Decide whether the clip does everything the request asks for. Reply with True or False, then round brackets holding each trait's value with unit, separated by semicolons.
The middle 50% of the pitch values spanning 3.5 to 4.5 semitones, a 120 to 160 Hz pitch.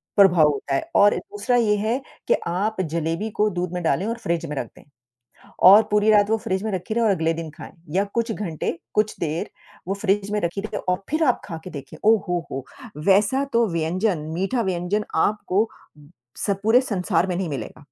False (4.0 semitones; 195 Hz)